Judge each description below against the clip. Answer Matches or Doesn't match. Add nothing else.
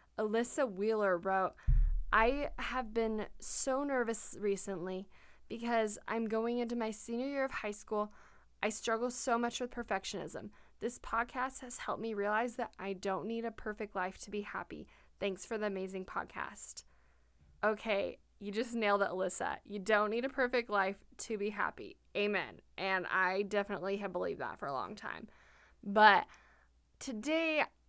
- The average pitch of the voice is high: Matches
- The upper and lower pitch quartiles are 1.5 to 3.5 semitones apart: Matches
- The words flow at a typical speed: Matches